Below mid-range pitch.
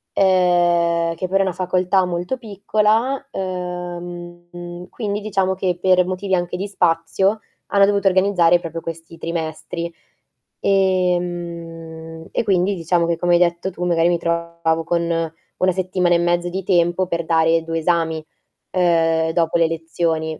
No: medium, 175 Hz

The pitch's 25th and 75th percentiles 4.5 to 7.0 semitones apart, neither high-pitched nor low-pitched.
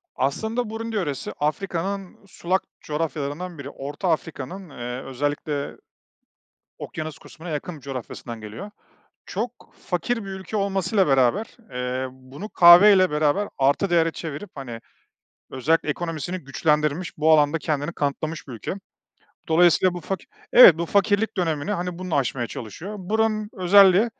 Yes: average, 5.1 semitones; medium, 165 Hz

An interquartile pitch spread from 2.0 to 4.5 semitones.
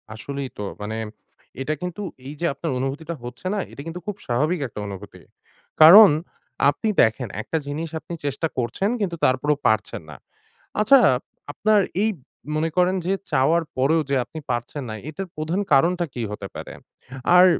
No: wide, 5.5 semitones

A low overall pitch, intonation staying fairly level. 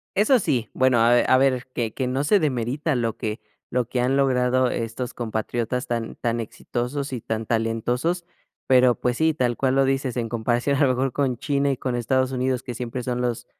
Yes: low, 125 Hz; narrow, 2.2 semitones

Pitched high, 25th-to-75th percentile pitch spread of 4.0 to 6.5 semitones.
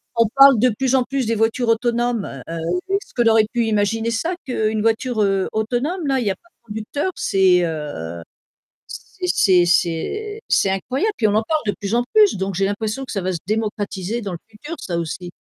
Yes: high, 220 Hz; average, 4.5 semitones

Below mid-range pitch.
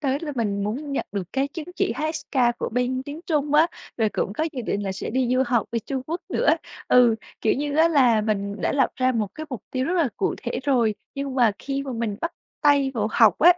No: very high, 260 Hz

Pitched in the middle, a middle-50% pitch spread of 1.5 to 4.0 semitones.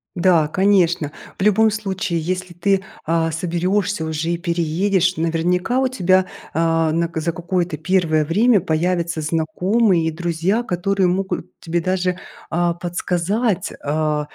Yes: medium, 175 Hz; narrow, 2.5 semitones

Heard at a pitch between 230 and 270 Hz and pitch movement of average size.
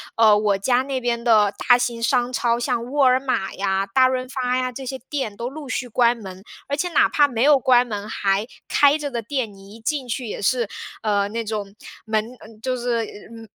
Yes: high, 240 Hz; average, 3.2 semitones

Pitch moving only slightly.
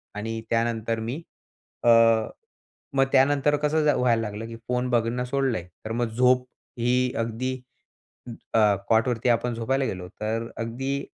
Yes: narrow, 2.2 semitones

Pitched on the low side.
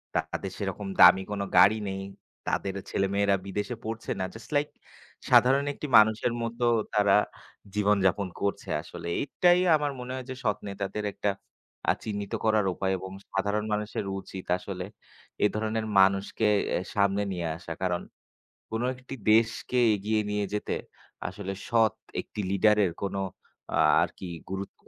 Yes: low, 105 Hz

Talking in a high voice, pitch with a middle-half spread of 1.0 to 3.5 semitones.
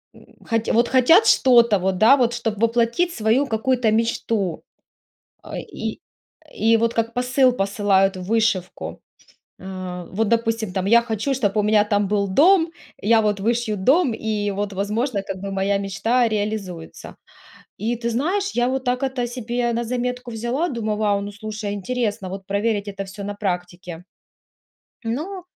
Yes: high, 220 Hz; average, 3.2 semitones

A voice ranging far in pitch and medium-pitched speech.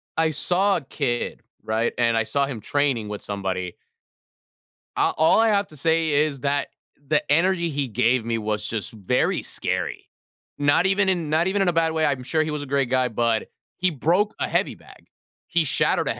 Yes: wide, 5.9 semitones; medium, 145 Hz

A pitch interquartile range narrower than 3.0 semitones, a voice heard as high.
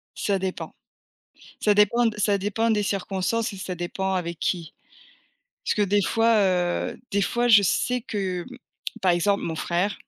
Yes: narrow, 2.6 semitones; high, 200 Hz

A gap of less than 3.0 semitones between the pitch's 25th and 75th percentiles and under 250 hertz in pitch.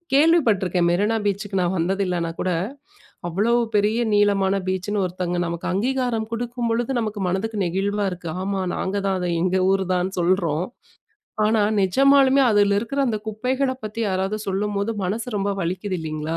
No: average, 3.3 semitones; high, 200 Hz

